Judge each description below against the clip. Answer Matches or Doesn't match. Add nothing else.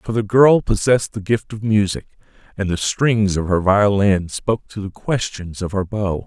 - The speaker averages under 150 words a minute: Doesn't match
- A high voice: Doesn't match